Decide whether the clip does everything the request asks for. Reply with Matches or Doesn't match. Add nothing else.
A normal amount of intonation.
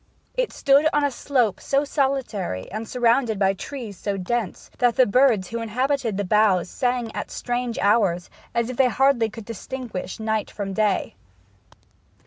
Matches